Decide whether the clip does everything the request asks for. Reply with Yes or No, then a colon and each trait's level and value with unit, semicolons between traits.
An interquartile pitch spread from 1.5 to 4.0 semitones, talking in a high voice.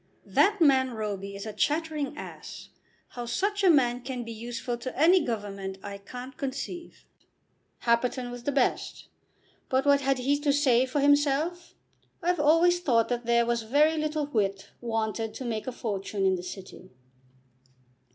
No: average, 4.5 semitones; very high, 255 Hz